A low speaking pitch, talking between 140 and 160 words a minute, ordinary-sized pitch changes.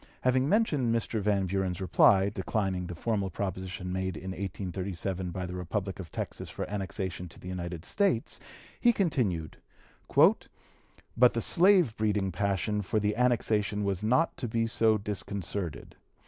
Yes: low, 100 Hz; average, 145 wpm; average, 3.4 semitones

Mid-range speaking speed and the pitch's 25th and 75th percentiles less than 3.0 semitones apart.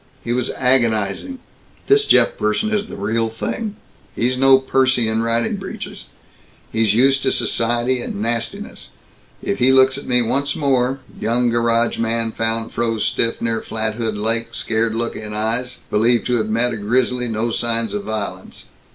Yes: average, 165 wpm; narrow, 2.4 semitones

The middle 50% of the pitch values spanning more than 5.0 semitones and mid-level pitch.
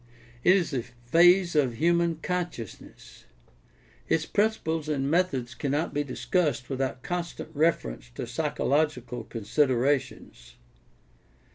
Yes: wide, 5.4 semitones; medium, 145 Hz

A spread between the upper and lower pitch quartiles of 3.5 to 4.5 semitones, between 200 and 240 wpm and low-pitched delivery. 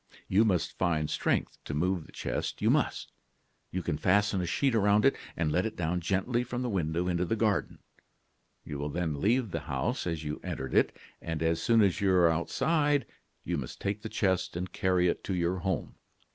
Yes: average, 3.8 semitones; fast, 205 wpm; very low, 90 Hz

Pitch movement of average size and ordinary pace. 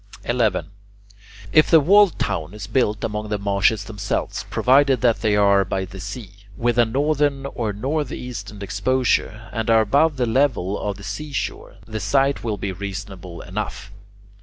Yes: average, 4.6 semitones; average, 160 wpm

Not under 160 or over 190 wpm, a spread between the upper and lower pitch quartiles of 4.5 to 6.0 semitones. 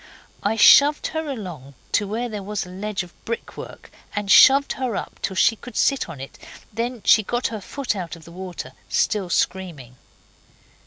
Yes: average, 180 wpm; average, 4.9 semitones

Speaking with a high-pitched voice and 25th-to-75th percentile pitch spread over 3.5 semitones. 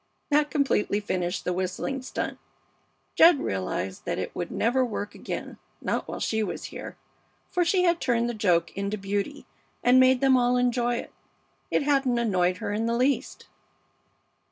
Yes: high, 240 Hz; average, 5.1 semitones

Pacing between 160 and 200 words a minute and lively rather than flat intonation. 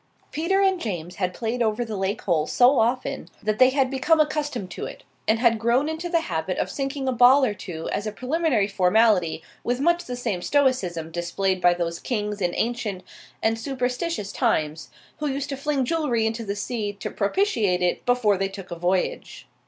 Yes: average, 195 wpm; wide, 5.9 semitones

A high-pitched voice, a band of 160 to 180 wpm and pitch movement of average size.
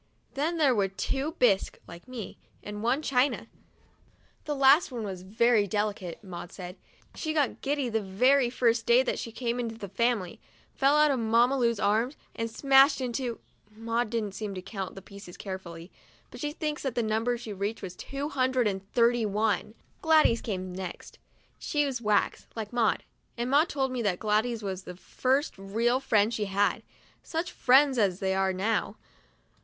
Yes: high, 230 Hz; average, 175 wpm; average, 4.6 semitones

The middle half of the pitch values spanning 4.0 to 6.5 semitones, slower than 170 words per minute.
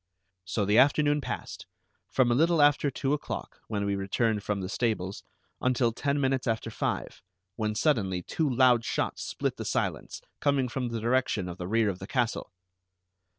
No: average, 4.6 semitones; average, 175 wpm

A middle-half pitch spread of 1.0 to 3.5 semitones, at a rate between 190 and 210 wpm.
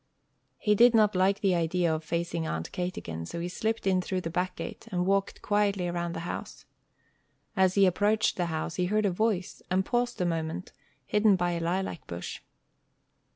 Yes: average, 2.8 semitones; average, 195 wpm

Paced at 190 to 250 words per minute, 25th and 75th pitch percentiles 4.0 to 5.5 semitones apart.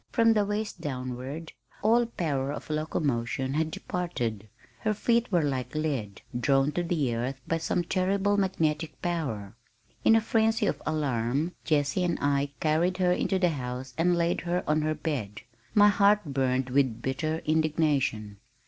No: average, 155 wpm; average, 5.2 semitones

